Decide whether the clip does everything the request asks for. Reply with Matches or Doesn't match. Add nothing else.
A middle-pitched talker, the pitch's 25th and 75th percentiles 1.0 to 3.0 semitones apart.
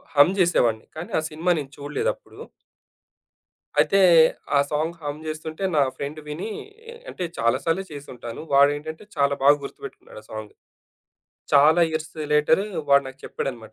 Matches